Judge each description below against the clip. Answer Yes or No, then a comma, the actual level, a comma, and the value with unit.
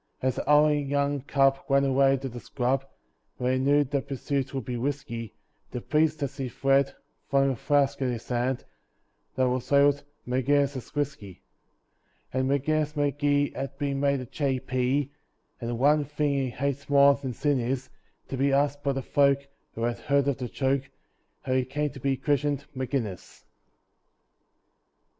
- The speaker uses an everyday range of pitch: No, narrow, 1.7 semitones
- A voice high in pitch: No, low, 135 Hz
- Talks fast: No, average, 170 wpm